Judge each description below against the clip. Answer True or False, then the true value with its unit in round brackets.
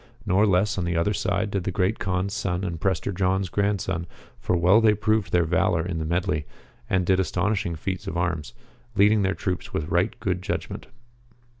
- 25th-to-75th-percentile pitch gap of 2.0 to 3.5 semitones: True (2.4 semitones)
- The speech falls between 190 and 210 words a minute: True (195 wpm)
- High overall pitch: False (95 Hz)